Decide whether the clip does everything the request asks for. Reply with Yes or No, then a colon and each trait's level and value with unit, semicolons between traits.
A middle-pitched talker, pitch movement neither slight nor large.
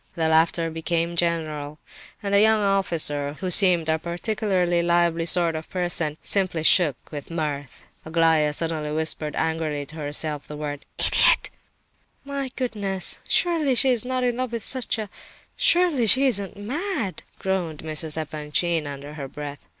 Yes: medium, 170 Hz; average, 4.7 semitones